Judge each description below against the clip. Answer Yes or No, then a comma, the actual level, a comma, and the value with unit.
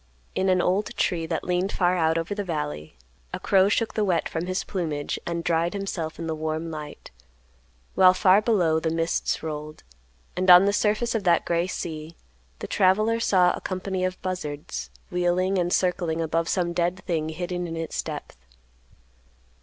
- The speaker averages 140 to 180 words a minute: Yes, average, 175 wpm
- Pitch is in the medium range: Yes, medium, 175 Hz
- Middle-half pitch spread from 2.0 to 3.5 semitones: Yes, narrow, 2.5 semitones